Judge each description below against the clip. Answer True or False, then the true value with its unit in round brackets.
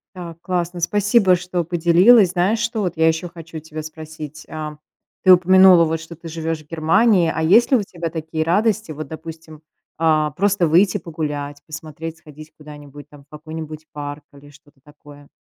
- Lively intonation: False (2.7 semitones)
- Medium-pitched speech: True (160 Hz)